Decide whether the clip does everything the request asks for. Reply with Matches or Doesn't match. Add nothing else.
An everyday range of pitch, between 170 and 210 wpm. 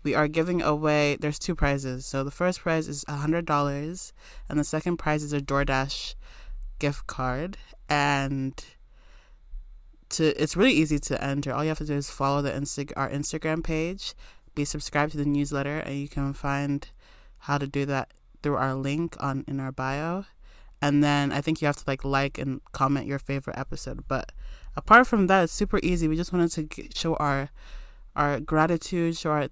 Doesn't match